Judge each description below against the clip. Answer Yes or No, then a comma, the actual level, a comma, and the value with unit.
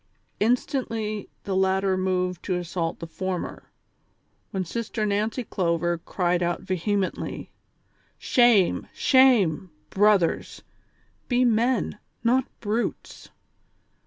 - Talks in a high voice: Yes, high, 195 Hz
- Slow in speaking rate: Yes, slow, 100 wpm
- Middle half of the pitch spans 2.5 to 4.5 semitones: Yes, average, 3.9 semitones